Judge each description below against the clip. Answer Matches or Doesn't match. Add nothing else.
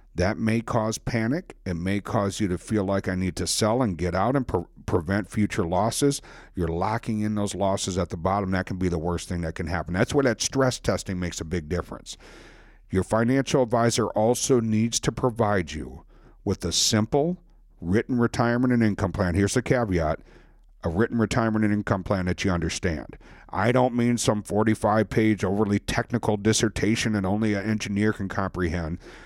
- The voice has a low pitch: Matches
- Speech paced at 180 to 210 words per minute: Matches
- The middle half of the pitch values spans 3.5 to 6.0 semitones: Matches